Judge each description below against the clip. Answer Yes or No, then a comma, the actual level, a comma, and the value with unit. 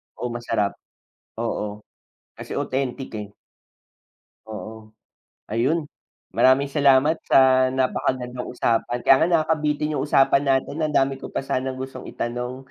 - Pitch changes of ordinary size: No, narrow, 2.3 semitones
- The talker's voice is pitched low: Yes, low, 130 Hz